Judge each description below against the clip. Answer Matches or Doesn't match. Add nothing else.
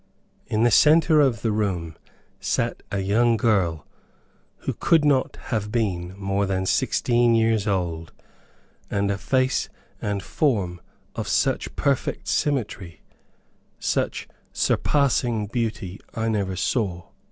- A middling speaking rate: Doesn't match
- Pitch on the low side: Matches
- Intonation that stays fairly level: Doesn't match